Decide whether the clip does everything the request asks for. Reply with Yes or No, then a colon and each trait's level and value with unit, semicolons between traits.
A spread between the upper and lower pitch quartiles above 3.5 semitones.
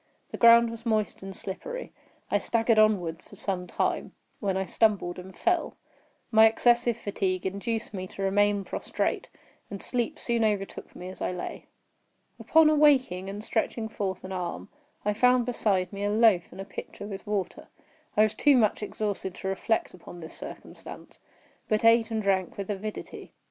No: average, 3.2 semitones